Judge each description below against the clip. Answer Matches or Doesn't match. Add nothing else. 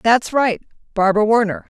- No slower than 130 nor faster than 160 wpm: Matches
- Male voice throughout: Doesn't match